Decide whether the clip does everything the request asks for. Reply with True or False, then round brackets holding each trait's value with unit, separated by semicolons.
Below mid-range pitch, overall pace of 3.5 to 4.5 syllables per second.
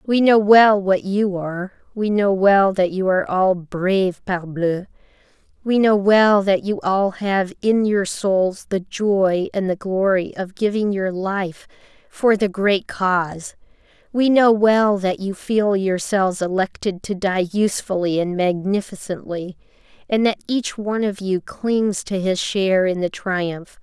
False (195 Hz; 4.0 syllables/s)